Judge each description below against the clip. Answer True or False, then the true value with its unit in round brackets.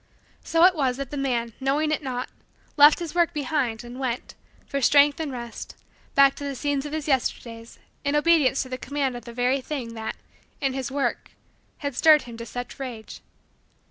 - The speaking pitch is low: False (270 Hz)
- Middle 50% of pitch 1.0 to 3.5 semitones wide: True (3.1 semitones)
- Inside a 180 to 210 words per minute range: True (195 wpm)